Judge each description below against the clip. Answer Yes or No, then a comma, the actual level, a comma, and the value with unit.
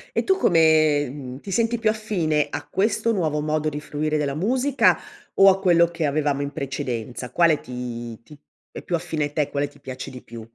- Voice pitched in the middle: Yes, medium, 150 Hz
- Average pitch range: Yes, average, 4.1 semitones